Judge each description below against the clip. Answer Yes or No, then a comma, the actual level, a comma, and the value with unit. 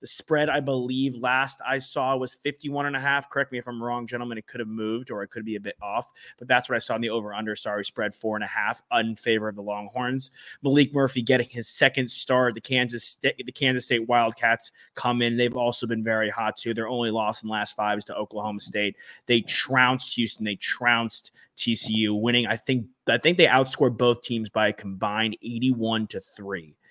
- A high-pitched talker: No, low, 120 Hz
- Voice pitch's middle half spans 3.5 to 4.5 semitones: No, average, 2.7 semitones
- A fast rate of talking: Yes, fast, 225 wpm